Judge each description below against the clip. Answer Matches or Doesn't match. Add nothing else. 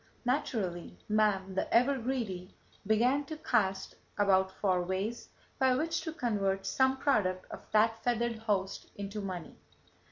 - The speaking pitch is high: Matches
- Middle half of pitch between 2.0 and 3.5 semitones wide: Doesn't match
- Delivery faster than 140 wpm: Doesn't match